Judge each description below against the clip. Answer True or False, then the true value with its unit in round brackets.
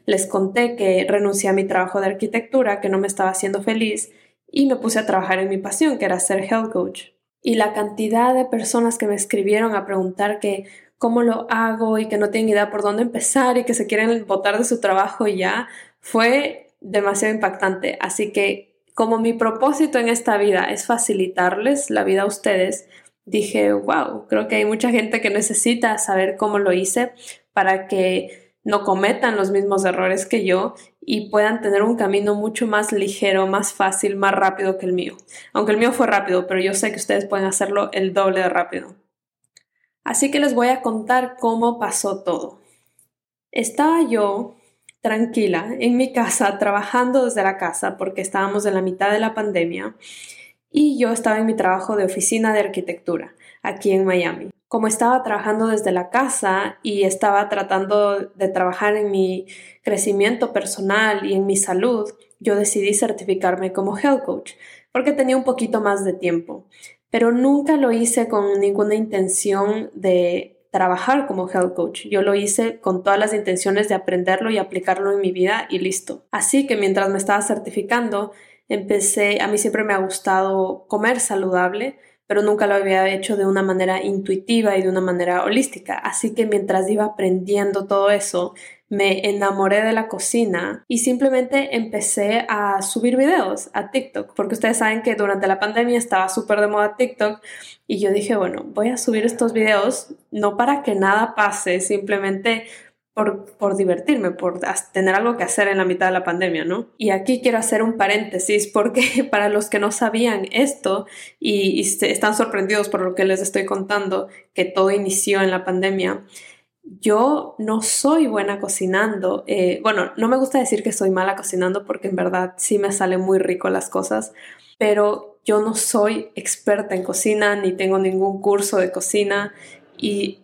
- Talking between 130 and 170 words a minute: False (180 wpm)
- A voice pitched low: False (205 Hz)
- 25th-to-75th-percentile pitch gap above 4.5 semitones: False (2.9 semitones)